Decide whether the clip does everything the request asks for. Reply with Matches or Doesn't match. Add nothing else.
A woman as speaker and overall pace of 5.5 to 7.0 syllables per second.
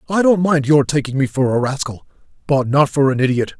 Doesn't match